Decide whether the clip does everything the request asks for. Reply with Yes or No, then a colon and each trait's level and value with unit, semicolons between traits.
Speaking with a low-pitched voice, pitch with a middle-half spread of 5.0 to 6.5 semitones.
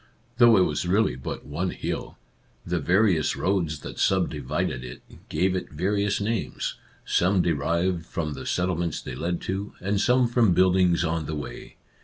No: very low, 90 Hz; average, 3.4 semitones